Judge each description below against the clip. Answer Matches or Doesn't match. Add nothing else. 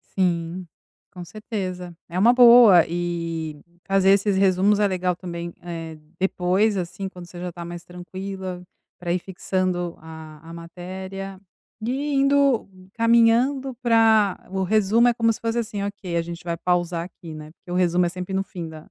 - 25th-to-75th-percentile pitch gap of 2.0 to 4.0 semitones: Matches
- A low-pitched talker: Doesn't match